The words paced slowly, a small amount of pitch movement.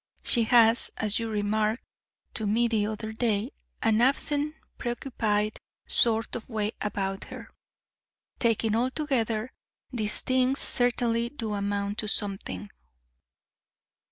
Yes: slow, 115 wpm; narrow, 2.3 semitones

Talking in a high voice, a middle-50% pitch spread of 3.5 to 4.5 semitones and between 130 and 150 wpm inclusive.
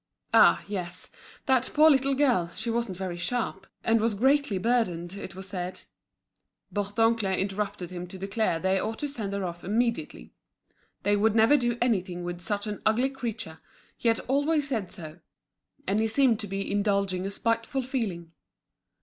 No: high, 205 Hz; average, 4.2 semitones; average, 165 wpm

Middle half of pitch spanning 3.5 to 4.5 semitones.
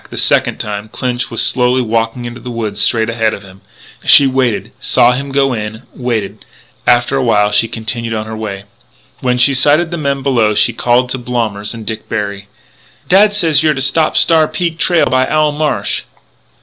Yes: average, 3.9 semitones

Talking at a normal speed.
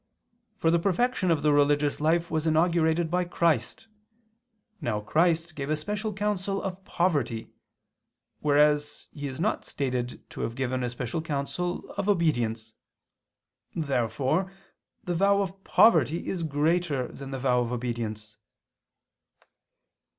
No: slow, 130 wpm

